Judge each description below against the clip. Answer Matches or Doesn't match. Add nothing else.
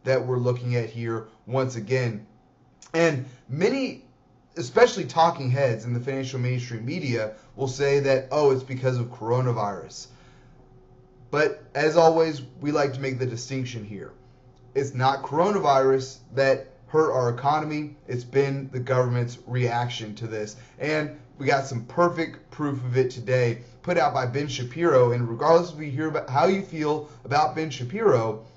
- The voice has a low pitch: Matches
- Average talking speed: Matches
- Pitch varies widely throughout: Doesn't match